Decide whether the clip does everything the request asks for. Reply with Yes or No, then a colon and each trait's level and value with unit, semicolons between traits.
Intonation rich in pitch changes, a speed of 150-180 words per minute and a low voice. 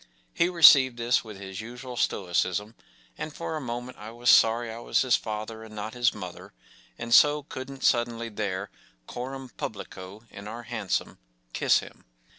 No: average, 3.1 semitones; average, 170 wpm; low, 115 Hz